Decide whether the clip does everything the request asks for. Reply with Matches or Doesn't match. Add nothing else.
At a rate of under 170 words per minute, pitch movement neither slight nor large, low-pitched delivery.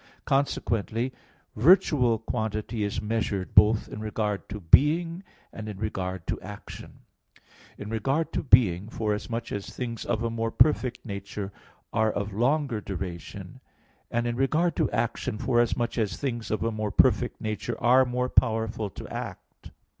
Matches